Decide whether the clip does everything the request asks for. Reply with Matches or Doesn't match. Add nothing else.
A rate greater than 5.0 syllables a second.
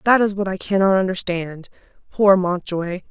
Doesn't match